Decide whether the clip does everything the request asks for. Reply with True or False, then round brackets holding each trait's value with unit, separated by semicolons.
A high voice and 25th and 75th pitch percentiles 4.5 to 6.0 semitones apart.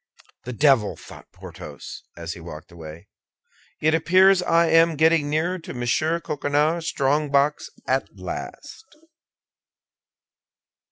False (150 Hz; 5.0 semitones)